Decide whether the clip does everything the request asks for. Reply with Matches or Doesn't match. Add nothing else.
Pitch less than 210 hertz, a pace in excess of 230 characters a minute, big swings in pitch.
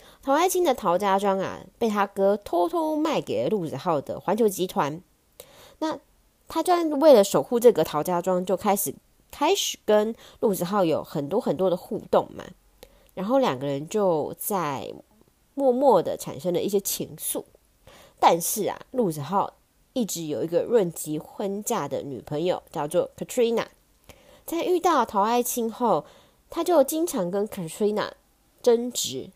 Doesn't match